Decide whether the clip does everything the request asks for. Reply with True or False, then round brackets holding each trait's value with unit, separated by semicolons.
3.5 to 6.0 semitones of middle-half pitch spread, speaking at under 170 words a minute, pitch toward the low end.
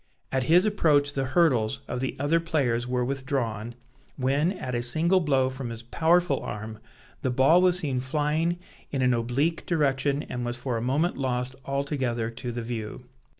False (3.9 semitones; 175 wpm; 130 Hz)